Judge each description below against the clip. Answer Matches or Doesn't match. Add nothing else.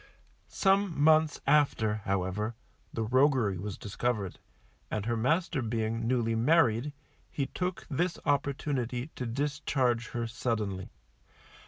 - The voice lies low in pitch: Matches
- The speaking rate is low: Matches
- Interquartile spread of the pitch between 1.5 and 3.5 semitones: Doesn't match